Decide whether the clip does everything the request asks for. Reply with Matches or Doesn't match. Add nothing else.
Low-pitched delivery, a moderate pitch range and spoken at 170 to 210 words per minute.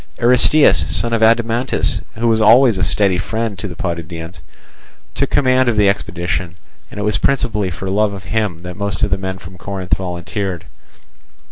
Matches